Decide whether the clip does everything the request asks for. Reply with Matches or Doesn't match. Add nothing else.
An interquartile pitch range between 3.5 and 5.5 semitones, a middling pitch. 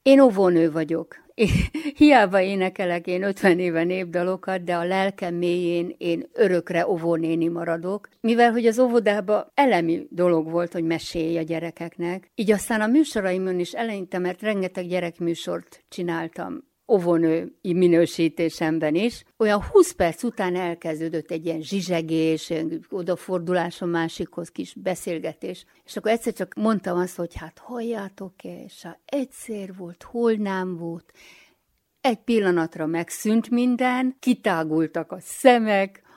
Matches